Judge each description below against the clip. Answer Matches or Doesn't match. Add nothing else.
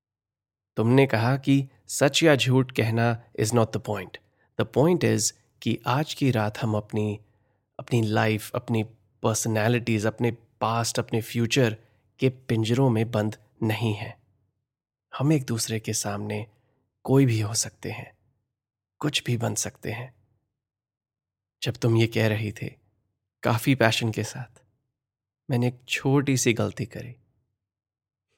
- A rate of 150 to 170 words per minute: Doesn't match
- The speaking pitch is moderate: Doesn't match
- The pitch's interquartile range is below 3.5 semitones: Matches